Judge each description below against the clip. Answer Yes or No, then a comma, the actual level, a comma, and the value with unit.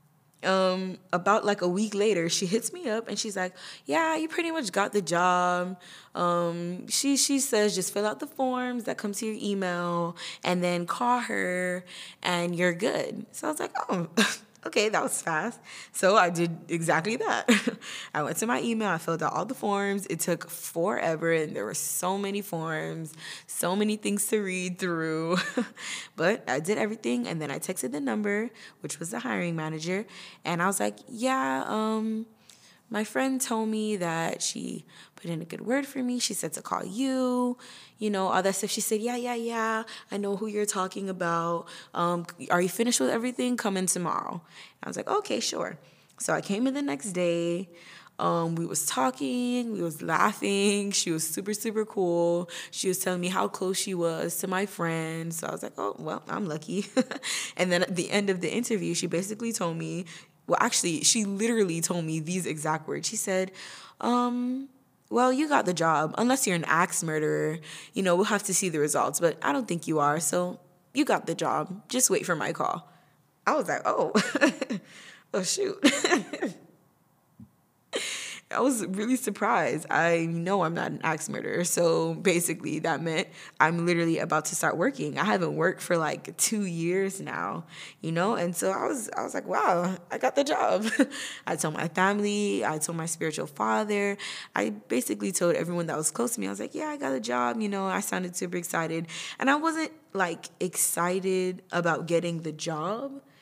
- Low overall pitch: No, medium, 185 Hz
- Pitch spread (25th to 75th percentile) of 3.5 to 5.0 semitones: Yes, average, 4.5 semitones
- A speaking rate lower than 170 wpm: No, average, 195 wpm